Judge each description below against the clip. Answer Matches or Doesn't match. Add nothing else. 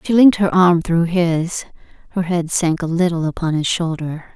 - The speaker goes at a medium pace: Matches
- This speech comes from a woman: Matches